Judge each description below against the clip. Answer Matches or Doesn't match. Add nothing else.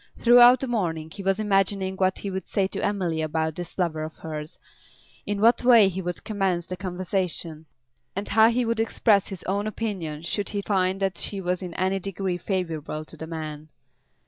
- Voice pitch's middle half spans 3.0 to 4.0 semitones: Matches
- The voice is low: Doesn't match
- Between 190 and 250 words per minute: Matches